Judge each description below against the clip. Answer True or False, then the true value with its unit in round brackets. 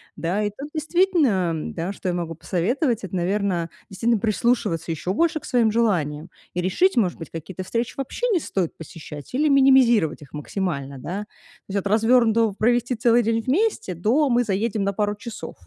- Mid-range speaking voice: False (210 Hz)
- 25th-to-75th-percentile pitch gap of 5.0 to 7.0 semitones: True (5.4 semitones)